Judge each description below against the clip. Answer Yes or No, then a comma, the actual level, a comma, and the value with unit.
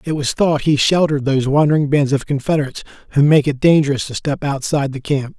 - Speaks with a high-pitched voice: No, medium, 145 Hz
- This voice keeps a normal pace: No, fast, 210 wpm